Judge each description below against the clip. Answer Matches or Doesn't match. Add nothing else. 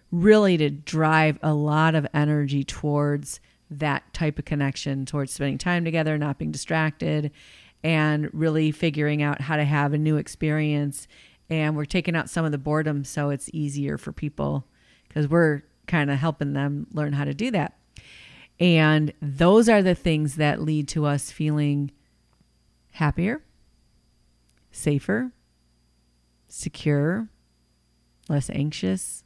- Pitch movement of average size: Doesn't match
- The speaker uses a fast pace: Doesn't match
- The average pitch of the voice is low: Doesn't match